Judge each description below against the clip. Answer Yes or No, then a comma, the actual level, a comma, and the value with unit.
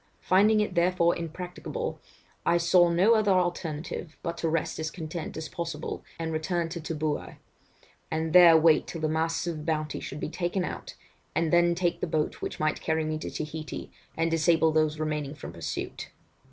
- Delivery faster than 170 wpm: Yes, average, 180 wpm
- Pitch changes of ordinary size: No, narrow, 1.8 semitones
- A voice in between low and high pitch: Yes, medium, 165 Hz